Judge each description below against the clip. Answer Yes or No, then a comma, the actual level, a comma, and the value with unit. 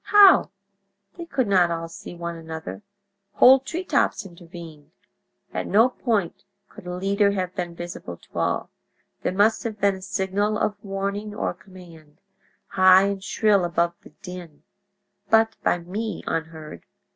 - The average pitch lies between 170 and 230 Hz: Yes, high, 190 Hz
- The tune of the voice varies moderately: Yes, average, 3.3 semitones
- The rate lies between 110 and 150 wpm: Yes, average, 145 wpm